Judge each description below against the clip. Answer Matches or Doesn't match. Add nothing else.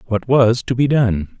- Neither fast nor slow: Doesn't match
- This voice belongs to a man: Matches